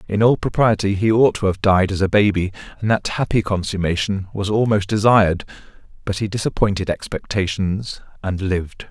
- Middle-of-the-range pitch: No, low, 100 Hz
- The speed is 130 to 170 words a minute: Yes, average, 160 wpm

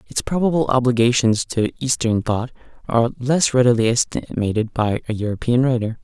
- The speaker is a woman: No, male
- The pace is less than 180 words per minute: Yes, average, 140 wpm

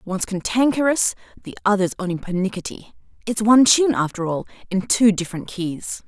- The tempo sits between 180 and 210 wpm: No, average, 150 wpm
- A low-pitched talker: No, high, 205 Hz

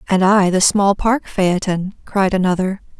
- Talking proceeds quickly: No, average, 160 wpm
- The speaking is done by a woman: Yes, female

